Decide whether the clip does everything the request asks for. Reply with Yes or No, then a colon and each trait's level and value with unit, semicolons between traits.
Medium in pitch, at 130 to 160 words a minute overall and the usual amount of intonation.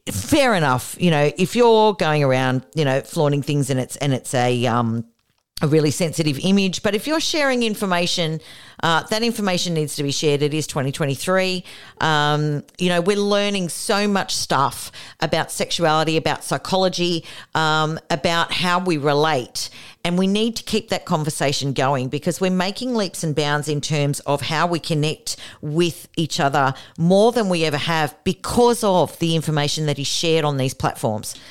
No: medium, 155 Hz; average, 175 wpm; average, 4.3 semitones